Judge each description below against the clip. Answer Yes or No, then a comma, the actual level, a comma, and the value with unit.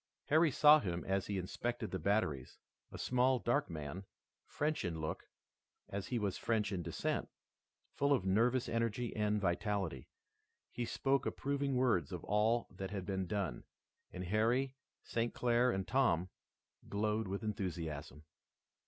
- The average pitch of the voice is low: Yes, low, 105 Hz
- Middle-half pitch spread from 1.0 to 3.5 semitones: No, average, 4.8 semitones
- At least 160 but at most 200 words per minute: No, average, 145 wpm